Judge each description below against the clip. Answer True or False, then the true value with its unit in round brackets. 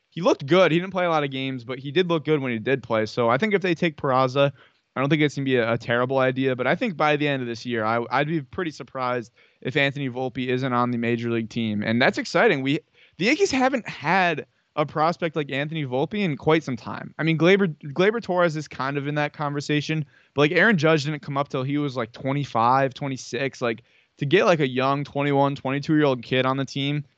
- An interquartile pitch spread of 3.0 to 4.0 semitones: True (3.5 semitones)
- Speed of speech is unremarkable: False (250 wpm)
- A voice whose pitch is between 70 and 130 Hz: False (140 Hz)